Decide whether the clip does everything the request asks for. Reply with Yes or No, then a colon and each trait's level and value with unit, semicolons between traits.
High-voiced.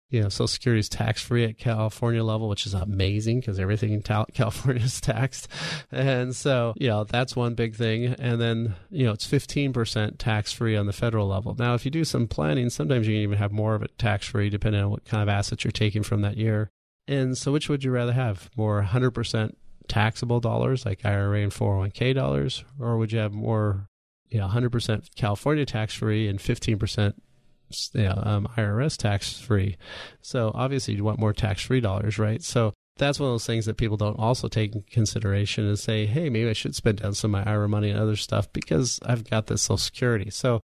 No: low, 110 Hz